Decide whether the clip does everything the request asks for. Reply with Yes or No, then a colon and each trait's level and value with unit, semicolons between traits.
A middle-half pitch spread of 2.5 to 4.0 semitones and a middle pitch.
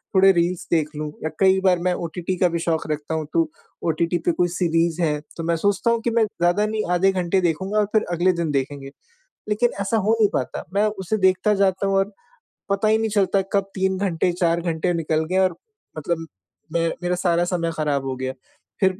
Yes: average, 2.8 semitones; medium, 180 Hz